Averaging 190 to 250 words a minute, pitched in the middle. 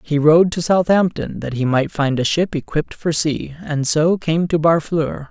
Yes: fast, 205 wpm; medium, 155 Hz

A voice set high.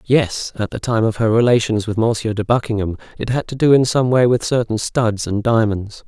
No: low, 115 Hz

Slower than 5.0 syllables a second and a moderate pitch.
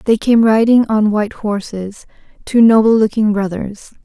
No: 4.7 syllables/s; high, 215 Hz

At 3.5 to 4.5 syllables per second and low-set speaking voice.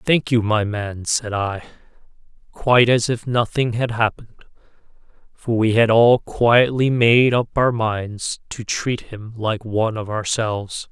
Yes: 4.1 syllables/s; low, 115 Hz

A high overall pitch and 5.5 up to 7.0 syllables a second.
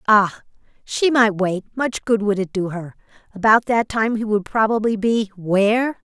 No: high, 215 Hz; 4.5 syllables/s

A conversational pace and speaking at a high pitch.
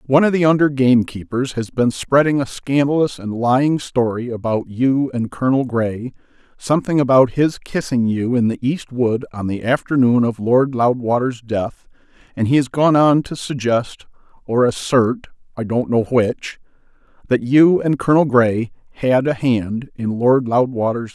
No: average, 160 wpm; low, 125 Hz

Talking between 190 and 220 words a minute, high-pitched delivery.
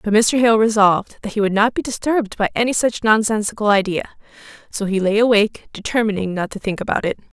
Yes: fast, 205 wpm; high, 215 Hz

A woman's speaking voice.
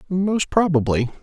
No: male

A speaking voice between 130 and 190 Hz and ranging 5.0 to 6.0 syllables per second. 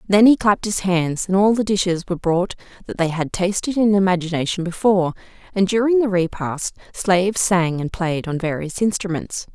Yes: medium, 185 Hz; 5.4 syllables/s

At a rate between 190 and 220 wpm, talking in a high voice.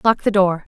No: fast, 235 wpm; high, 195 Hz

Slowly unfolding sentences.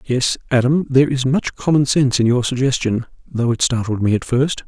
No: fast, 205 wpm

